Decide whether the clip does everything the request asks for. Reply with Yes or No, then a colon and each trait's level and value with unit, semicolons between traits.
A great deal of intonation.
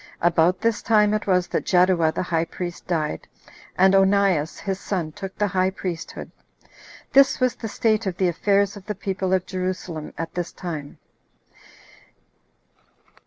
No: narrow, 2.6 semitones